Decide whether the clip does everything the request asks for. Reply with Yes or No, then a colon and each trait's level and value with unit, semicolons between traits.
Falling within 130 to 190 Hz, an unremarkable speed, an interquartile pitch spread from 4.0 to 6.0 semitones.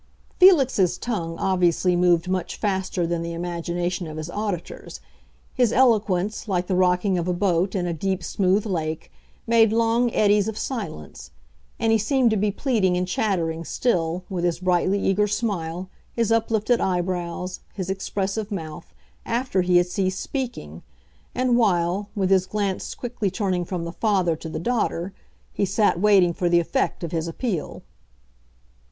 No: medium, 185 Hz; average, 160 wpm; average, 3.5 semitones